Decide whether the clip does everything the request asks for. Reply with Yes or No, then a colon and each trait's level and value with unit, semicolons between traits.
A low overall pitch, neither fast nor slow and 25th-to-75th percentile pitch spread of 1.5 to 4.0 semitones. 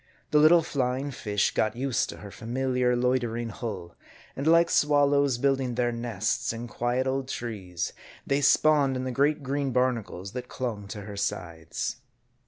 Yes: low, 125 Hz; average, 160 wpm; average, 3.4 semitones